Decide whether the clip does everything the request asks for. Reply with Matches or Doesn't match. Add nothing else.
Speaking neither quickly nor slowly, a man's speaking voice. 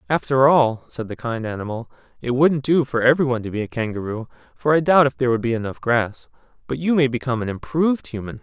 Doesn't match